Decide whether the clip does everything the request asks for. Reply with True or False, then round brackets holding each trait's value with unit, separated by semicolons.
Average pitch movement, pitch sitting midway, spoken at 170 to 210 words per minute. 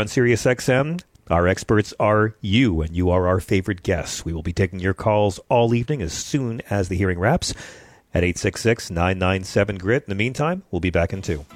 False (4.3 semitones; 100 Hz; 200 wpm)